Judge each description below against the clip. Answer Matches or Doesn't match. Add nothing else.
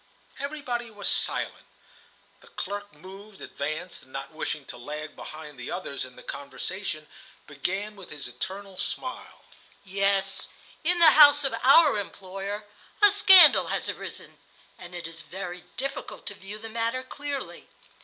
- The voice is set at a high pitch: Matches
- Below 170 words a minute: Matches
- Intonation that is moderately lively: Doesn't match